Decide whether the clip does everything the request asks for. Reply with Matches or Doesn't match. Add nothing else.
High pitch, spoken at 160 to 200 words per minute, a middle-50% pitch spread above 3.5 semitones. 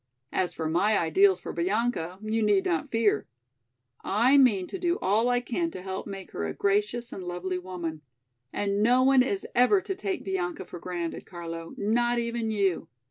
Matches